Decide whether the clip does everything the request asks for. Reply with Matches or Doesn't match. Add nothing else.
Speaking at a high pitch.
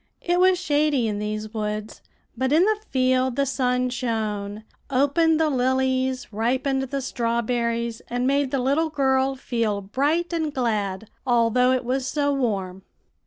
Matches